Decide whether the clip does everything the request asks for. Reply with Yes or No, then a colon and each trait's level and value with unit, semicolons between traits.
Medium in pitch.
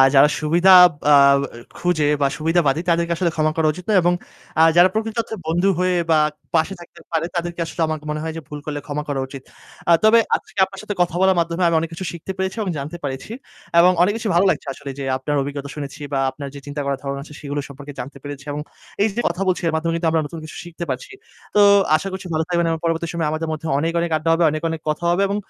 Yes: medium, 165 Hz